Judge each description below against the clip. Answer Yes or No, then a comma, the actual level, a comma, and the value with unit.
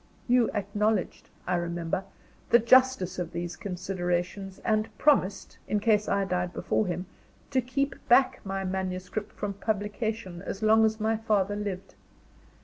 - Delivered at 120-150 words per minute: Yes, average, 140 wpm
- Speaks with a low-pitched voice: No, high, 200 Hz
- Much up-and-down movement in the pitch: No, average, 3.2 semitones